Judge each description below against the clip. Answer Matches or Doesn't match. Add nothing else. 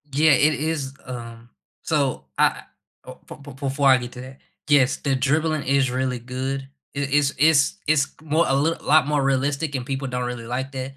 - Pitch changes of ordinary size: Doesn't match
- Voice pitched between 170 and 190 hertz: Doesn't match